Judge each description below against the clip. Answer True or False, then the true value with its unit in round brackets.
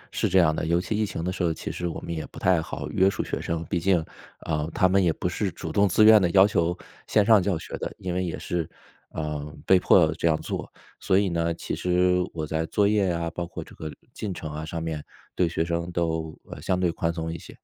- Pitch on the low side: True (85 Hz)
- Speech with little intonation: True (2.3 semitones)